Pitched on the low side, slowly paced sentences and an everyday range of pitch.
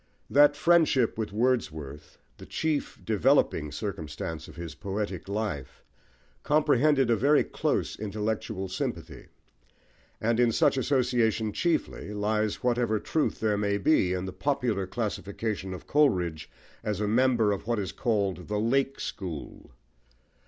Yes: low, 110 Hz; slow, 130 wpm; average, 4.6 semitones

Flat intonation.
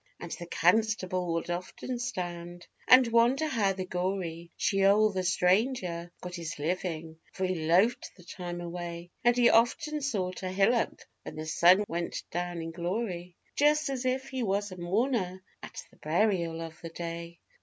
No: average, 4.5 semitones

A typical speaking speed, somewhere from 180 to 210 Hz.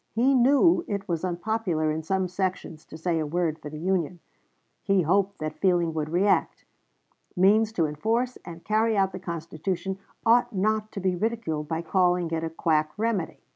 Yes: average, 175 wpm; medium, 185 Hz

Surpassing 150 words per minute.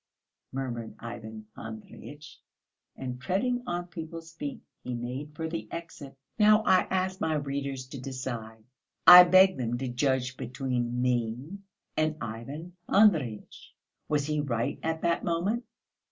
No: slow, 135 wpm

